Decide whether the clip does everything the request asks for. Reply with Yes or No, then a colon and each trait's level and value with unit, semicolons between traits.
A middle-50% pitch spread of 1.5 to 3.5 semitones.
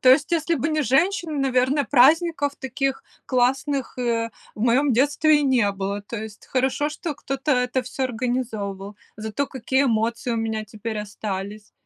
No: average, 4.3 semitones